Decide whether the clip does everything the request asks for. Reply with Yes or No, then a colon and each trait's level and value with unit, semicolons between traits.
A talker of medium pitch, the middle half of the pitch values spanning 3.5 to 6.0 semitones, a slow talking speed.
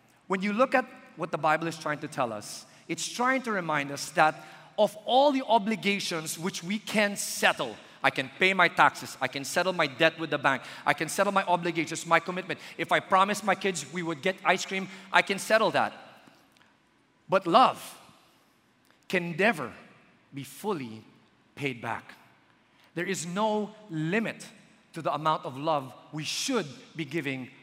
No: medium, 175 Hz; average, 4.7 semitones; average, 175 wpm